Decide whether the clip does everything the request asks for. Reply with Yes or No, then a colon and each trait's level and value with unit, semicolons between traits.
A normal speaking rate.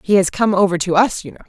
No: fast, 325 wpm